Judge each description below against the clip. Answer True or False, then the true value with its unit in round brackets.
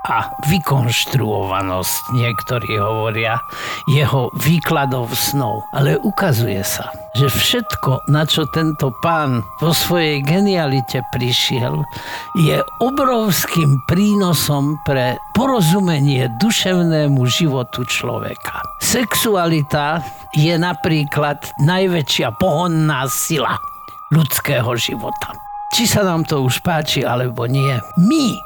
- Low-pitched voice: False (145 Hz)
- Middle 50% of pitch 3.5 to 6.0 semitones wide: True (5.2 semitones)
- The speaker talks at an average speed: False (95 wpm)